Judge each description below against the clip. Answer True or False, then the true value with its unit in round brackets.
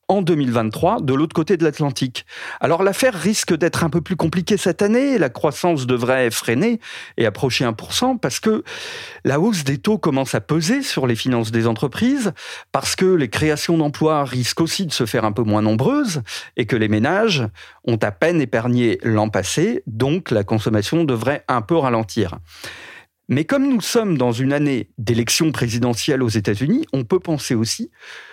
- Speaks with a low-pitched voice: False (145 Hz)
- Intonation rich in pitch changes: True (7.5 semitones)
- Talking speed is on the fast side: False (180 wpm)